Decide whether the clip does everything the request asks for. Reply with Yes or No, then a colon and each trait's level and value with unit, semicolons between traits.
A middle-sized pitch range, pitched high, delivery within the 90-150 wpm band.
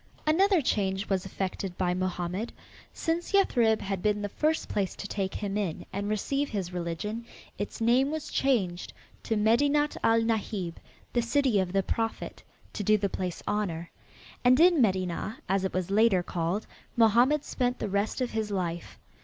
No: average, 4.3 semitones; high, 210 Hz; average, 170 wpm